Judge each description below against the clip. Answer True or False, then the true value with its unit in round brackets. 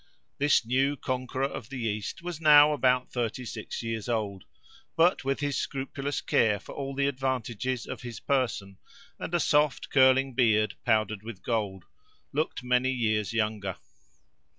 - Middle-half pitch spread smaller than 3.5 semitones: False (3.8 semitones)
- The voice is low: True (125 Hz)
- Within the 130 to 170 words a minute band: True (150 wpm)